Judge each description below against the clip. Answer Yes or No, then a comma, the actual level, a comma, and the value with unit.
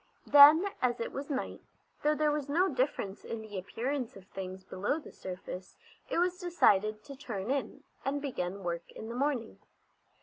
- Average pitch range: No, wide, 6.8 semitones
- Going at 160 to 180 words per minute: Yes, average, 175 wpm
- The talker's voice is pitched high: Yes, very high, 250 Hz